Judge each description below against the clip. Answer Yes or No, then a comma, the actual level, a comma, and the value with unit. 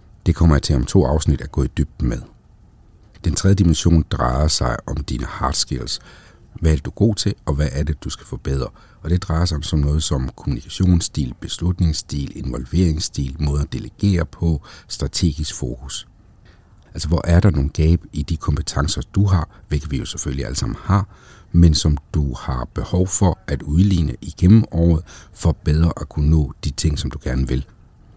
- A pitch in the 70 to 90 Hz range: Yes, very low, 80 Hz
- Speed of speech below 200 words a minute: Yes, average, 190 wpm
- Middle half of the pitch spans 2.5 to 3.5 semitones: No, average, 4.0 semitones